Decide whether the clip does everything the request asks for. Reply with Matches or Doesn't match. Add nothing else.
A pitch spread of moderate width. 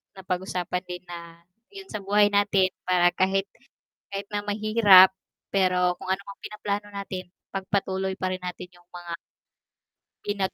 Doesn't match